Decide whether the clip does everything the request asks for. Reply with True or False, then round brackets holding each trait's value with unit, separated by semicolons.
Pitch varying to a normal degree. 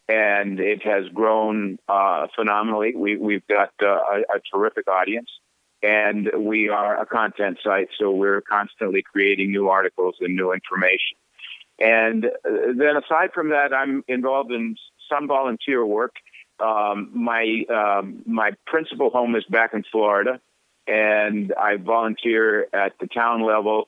False (2.2 semitones)